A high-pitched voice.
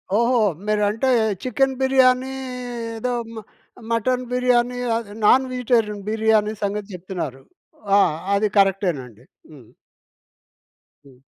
Yes: high, 220 Hz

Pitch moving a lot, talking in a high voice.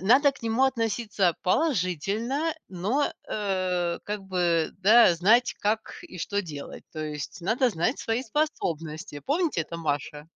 Yes: wide, 6.0 semitones; high, 200 Hz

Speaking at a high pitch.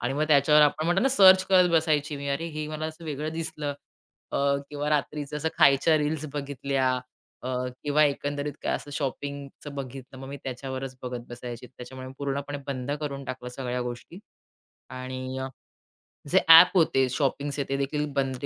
No: medium, 140 Hz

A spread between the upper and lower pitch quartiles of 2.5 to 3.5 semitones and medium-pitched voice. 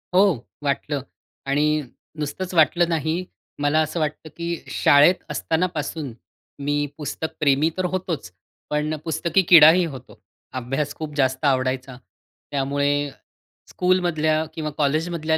Yes: average, 3.0 semitones; medium, 155 Hz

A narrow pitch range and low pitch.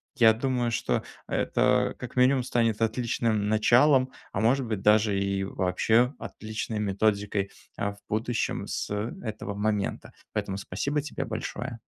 No: average, 3.1 semitones; low, 110 Hz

